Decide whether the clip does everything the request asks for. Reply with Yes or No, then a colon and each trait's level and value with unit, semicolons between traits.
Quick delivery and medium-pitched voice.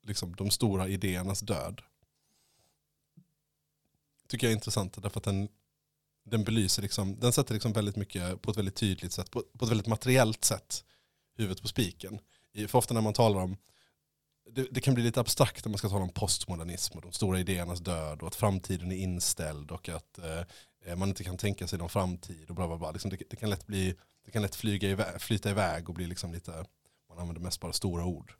No: fast, 205 wpm; low, 100 Hz